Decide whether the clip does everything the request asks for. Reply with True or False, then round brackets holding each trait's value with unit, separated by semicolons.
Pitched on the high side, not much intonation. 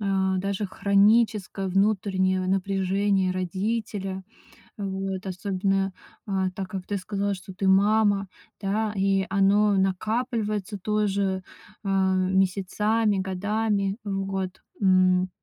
True (195 Hz; 1.4 semitones)